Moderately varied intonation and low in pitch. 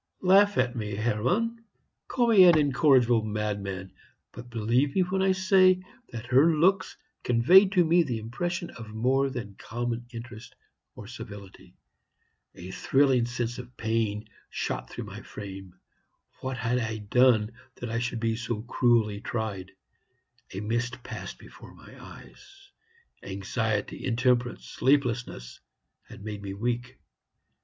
Yes: average, 4.4 semitones; low, 120 Hz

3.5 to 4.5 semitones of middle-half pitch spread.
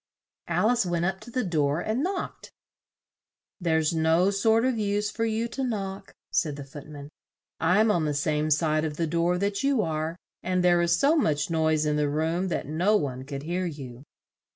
No: average, 5.2 semitones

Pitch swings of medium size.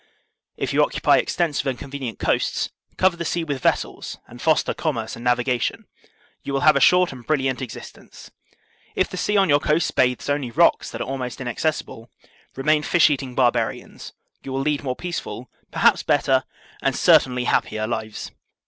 Yes: average, 3.9 semitones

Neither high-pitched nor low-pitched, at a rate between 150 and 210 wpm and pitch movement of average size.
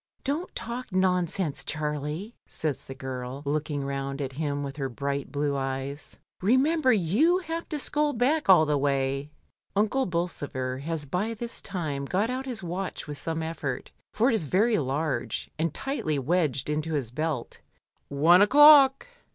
No: medium, 160 Hz; average, 160 wpm; wide, 7.7 semitones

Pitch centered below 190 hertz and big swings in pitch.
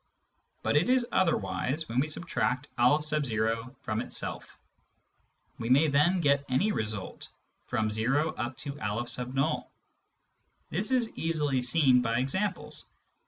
No: medium, 140 Hz; average, 5.0 semitones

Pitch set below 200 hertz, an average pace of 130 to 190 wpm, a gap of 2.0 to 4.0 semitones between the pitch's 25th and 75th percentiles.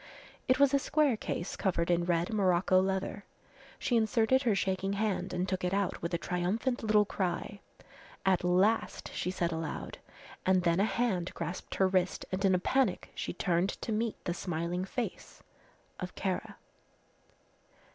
Yes: high, 190 Hz; average, 165 wpm; average, 3.4 semitones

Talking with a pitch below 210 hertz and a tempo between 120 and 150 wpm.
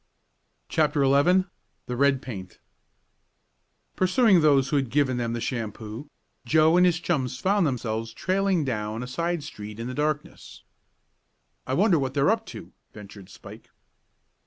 Yes: medium, 140 Hz; average, 145 wpm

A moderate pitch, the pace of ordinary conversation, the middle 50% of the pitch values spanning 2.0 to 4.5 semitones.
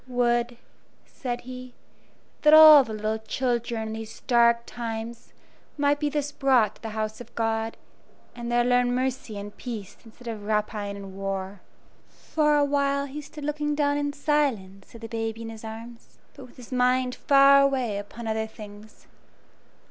No: high, 240 Hz; average, 170 wpm; average, 3.8 semitones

